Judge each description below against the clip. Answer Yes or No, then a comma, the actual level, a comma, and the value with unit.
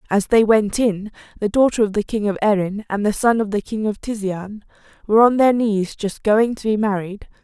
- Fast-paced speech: Yes, fast, 225 wpm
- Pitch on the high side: Yes, high, 210 Hz